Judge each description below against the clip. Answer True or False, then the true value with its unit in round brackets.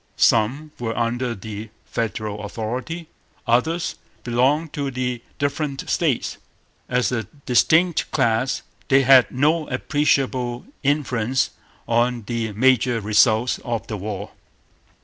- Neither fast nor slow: False (110 wpm)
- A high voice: False (125 Hz)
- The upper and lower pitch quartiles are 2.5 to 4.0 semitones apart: True (3.3 semitones)